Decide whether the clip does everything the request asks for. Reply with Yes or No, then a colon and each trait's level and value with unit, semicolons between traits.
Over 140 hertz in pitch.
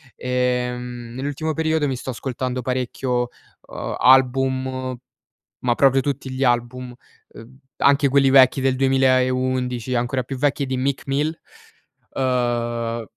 No: low, 130 Hz